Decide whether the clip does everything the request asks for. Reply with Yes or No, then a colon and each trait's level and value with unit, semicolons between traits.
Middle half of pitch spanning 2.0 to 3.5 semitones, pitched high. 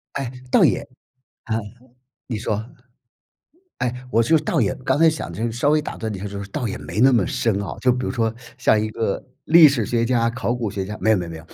No: average, 3.2 semitones; low, 115 Hz